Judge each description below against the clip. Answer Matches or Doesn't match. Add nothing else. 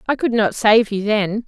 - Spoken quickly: Matches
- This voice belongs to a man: Doesn't match